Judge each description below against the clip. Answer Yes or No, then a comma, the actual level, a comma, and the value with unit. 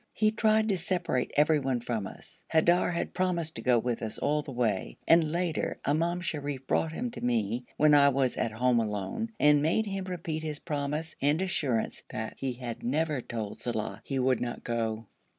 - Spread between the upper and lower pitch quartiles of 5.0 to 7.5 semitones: Yes, wide, 5.5 semitones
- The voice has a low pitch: No, medium, 145 Hz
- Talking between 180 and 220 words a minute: Yes, average, 190 wpm